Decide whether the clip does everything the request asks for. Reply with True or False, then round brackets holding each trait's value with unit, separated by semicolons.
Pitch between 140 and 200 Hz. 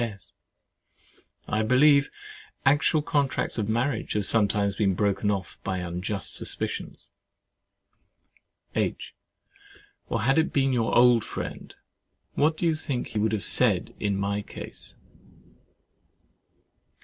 False (110 Hz)